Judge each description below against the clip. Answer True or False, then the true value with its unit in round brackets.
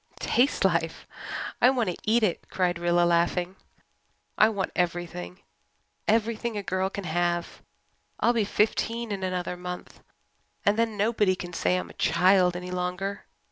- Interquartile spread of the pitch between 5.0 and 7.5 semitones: False (3.3 semitones)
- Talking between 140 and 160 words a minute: True (150 wpm)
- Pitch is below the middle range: False (185 Hz)